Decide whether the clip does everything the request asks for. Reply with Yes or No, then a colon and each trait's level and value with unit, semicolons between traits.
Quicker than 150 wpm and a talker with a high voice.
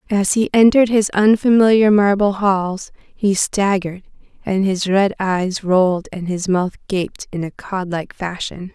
Yes: average, 160 wpm; high, 195 Hz